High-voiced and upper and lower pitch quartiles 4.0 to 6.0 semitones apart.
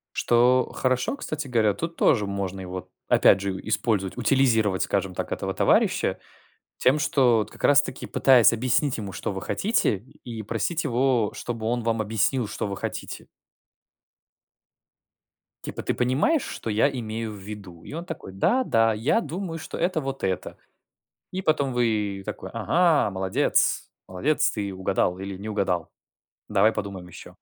No: low, 115 Hz; average, 5.2 semitones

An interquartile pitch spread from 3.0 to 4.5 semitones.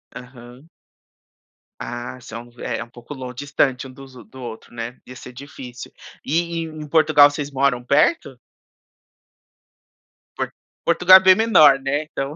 Yes: average, 3.4 semitones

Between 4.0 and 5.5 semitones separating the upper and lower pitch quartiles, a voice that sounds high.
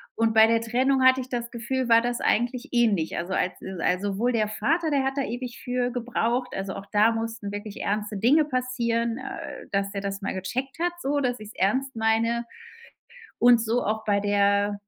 No: average, 3.4 semitones; high, 230 Hz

